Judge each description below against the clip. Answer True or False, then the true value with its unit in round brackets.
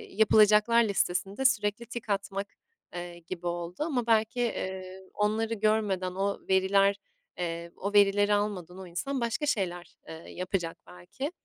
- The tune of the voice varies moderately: True (3.2 semitones)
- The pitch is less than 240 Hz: True (200 Hz)